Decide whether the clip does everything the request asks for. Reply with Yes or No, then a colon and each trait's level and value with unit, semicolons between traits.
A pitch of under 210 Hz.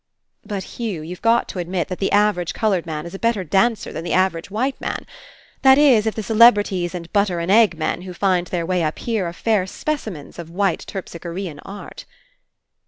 Yes: high, 190 Hz